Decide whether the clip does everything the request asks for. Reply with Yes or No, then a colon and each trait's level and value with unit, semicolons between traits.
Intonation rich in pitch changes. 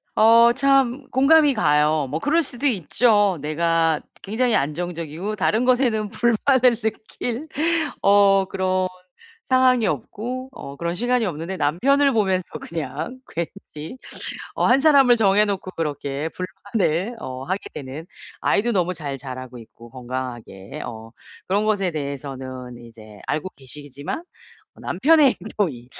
Yes: wide, 8.6 semitones